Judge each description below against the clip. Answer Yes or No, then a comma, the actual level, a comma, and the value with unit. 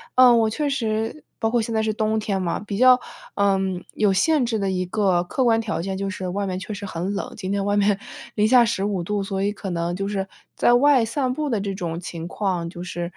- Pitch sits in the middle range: No, high, 205 Hz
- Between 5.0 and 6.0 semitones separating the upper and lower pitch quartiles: No, average, 2.9 semitones